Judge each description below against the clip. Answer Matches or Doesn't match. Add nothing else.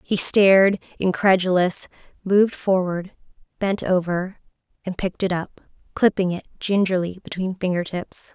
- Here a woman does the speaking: Matches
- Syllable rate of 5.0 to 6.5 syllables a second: Doesn't match